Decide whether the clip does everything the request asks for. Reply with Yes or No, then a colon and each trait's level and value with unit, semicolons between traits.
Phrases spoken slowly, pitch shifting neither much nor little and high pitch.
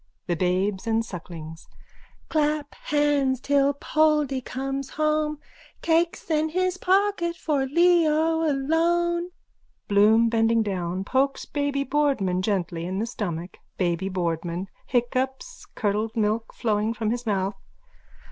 No: slow, 120 wpm; wide, 7.2 semitones; very high, 260 Hz